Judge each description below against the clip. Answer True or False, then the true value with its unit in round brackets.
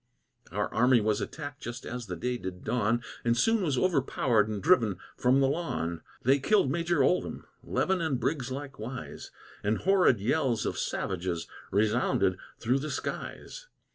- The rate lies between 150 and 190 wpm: True (155 wpm)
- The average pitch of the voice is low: True (125 Hz)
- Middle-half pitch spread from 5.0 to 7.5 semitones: True (5.5 semitones)